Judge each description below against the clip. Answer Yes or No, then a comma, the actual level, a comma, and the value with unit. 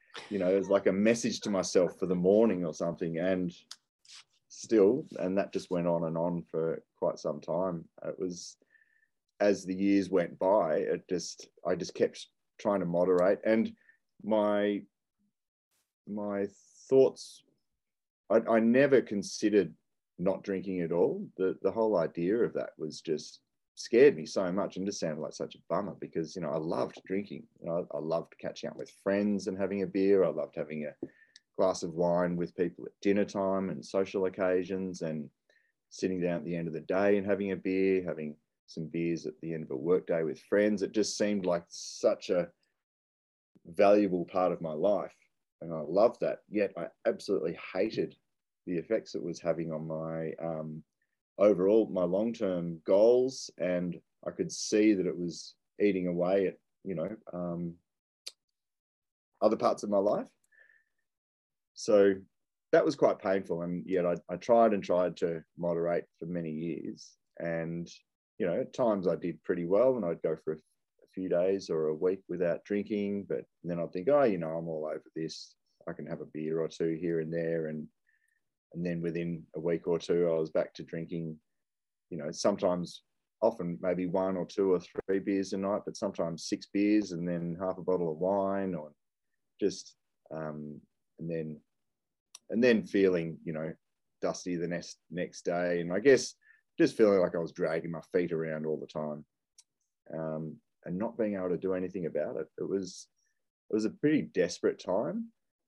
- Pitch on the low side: Yes, very low, 90 Hz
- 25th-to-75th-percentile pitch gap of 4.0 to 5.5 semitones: No, average, 3.2 semitones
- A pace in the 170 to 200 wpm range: Yes, average, 185 wpm